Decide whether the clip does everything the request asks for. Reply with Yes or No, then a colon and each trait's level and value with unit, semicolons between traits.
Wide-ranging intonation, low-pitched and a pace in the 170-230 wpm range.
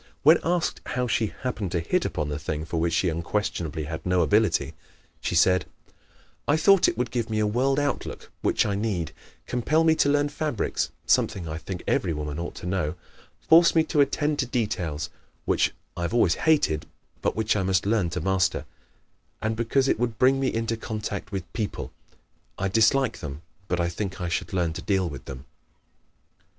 Yes: wide, 6.7 semitones; low, 105 Hz; average, 190 wpm